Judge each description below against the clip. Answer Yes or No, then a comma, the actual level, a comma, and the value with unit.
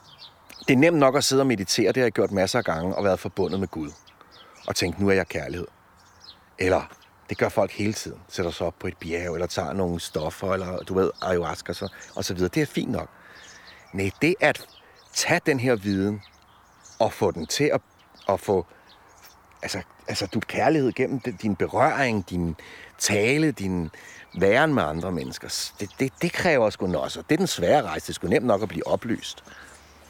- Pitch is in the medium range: No, very low, 95 Hz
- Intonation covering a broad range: Yes, wide, 6.1 semitones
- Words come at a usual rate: Yes, average, 205 wpm